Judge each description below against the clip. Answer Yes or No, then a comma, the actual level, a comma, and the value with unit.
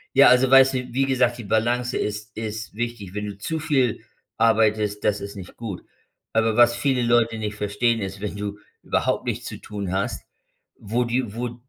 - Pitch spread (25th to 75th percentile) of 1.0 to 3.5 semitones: Yes, average, 2.9 semitones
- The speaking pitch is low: Yes, low, 115 Hz